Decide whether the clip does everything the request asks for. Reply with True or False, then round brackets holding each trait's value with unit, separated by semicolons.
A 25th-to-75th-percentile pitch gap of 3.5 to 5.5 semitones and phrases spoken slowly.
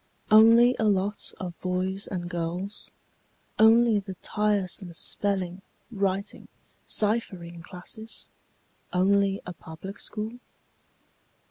False (2.7 semitones; 95 wpm)